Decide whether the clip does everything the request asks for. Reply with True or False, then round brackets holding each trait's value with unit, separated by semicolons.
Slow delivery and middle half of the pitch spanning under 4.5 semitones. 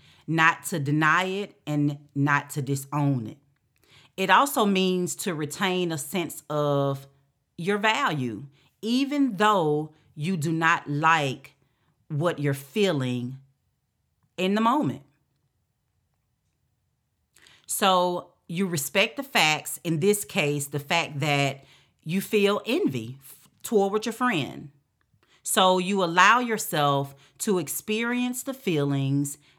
False (115 wpm; 5.3 semitones)